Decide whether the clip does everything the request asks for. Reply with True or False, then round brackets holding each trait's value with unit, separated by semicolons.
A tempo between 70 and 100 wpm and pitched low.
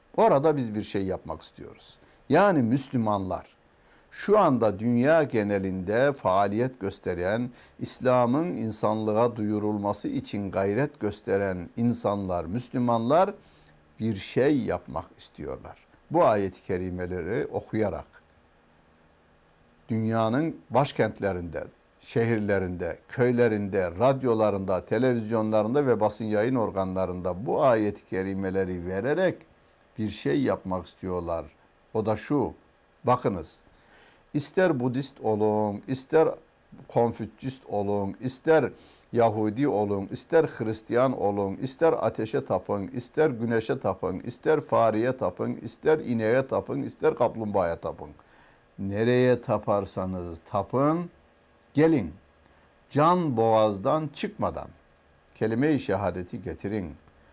True (95 wpm; 105 Hz)